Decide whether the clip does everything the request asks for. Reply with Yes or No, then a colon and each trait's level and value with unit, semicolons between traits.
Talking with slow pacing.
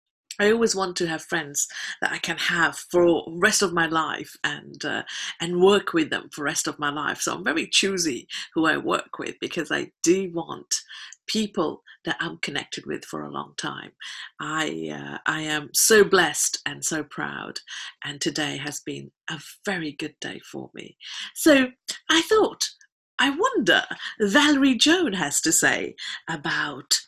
No: average, 175 wpm